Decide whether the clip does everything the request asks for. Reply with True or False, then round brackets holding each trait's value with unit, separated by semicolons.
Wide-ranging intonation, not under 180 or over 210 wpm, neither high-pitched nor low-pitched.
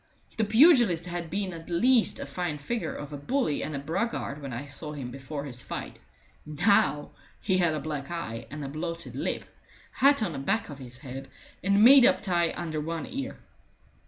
True (5.8 semitones; 195 wpm; 165 Hz)